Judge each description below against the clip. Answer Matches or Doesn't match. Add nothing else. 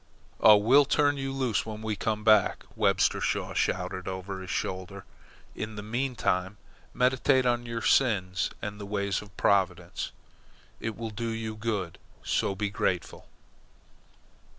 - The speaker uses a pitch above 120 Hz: Doesn't match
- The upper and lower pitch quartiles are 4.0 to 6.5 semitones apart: Doesn't match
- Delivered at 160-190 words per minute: Doesn't match